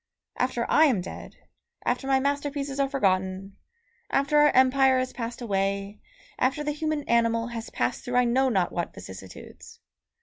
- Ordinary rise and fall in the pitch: No, wide, 5.7 semitones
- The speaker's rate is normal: Yes, average, 160 wpm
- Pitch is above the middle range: Yes, very high, 250 Hz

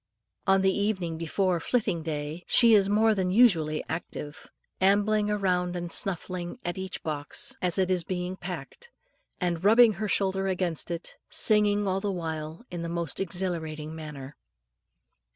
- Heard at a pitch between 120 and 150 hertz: No, medium, 180 Hz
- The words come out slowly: No, average, 150 wpm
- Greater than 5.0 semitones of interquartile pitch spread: No, average, 3.2 semitones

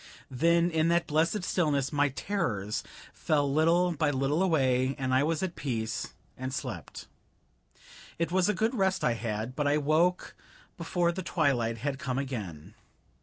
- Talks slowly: No, average, 160 wpm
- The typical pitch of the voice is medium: Yes, medium, 150 Hz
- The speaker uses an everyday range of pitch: Yes, average, 4.7 semitones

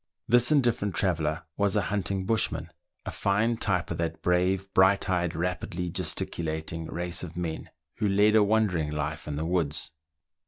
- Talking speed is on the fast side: No, average, 160 wpm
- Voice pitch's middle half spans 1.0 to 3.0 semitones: No, average, 3.6 semitones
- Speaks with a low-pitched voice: Yes, very low, 90 Hz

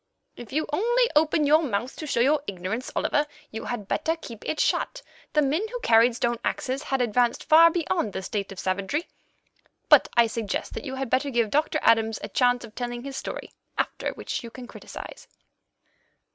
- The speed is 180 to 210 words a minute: Yes, average, 190 wpm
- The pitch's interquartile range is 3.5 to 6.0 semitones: Yes, average, 4.9 semitones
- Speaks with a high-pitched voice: Yes, very high, 250 Hz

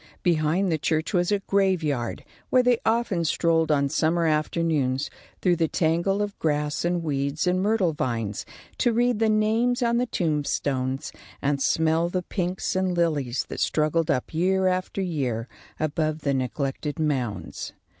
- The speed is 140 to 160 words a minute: Yes, average, 155 wpm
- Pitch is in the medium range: Yes, medium, 165 Hz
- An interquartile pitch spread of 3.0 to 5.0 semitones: Yes, average, 4.3 semitones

